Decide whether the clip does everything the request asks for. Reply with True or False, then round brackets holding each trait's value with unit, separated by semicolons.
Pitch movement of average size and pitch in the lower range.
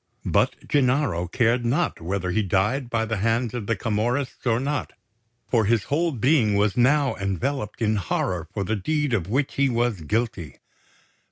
True (4.5 semitones; 115 Hz)